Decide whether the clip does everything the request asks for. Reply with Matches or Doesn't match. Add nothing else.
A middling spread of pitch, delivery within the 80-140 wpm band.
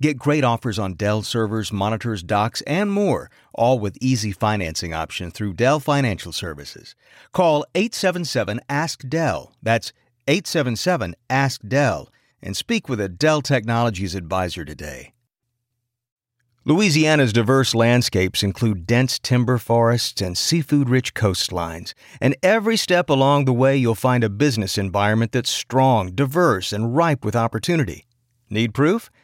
Matches